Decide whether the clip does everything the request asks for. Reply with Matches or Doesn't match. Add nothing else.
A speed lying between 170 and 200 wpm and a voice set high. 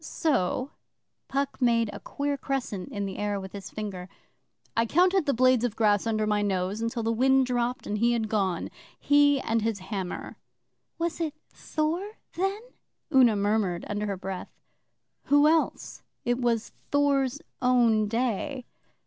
Doesn't match